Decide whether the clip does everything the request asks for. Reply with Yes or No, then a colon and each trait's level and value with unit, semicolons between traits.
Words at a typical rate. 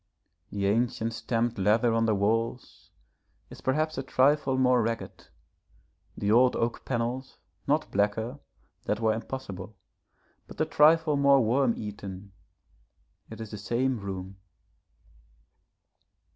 No: slow, 120 wpm